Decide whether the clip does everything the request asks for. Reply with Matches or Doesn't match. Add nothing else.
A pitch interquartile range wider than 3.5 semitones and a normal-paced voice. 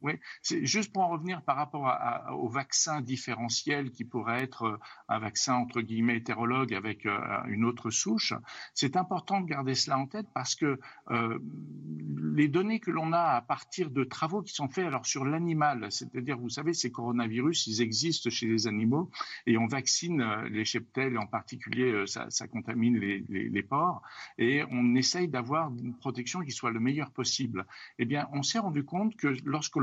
Matches